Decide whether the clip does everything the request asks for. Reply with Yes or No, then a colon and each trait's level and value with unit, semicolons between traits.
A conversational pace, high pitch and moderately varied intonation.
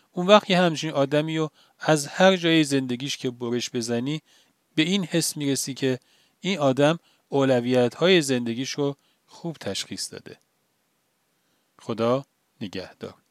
No: average, 130 wpm; medium, 145 Hz; average, 4.4 semitones